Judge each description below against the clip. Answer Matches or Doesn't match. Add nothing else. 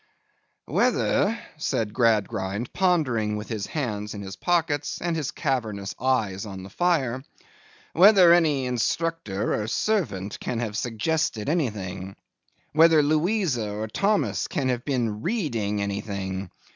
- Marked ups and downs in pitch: Matches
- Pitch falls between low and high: Doesn't match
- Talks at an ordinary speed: Doesn't match